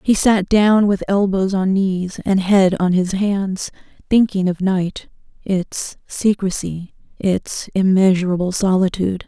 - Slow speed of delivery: Yes, slow, 130 wpm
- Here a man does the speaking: No, female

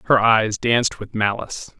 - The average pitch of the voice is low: Yes, low, 115 Hz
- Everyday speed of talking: Yes, average, 165 wpm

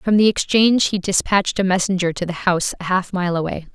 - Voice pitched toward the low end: No, medium, 185 Hz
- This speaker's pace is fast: Yes, fast, 225 wpm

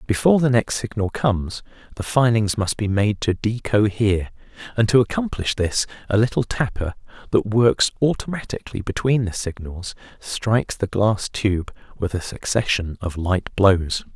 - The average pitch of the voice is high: No, low, 105 Hz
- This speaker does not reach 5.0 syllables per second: Yes, 4.8 syllables/s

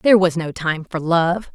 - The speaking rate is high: Yes, fast, 235 wpm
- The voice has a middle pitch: Yes, medium, 175 Hz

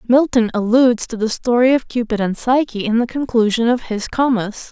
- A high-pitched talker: Yes, high, 235 Hz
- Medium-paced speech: Yes, average, 190 wpm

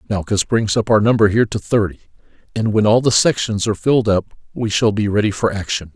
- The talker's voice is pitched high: No, low, 105 Hz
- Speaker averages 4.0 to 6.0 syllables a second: No, 6.3 syllables/s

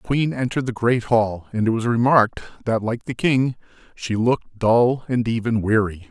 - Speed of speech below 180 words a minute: No, average, 195 wpm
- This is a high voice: No, low, 115 Hz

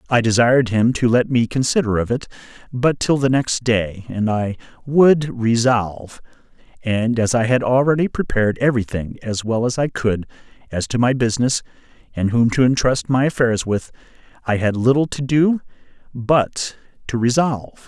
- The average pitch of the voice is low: Yes, low, 120 Hz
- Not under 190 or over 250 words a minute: No, average, 165 wpm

